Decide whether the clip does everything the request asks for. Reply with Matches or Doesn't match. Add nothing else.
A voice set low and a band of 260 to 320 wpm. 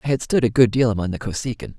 Matches